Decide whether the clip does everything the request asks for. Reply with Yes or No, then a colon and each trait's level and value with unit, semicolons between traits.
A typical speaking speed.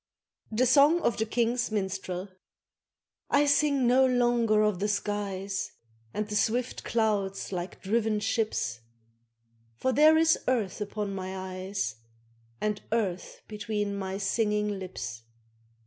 No: slow, 125 wpm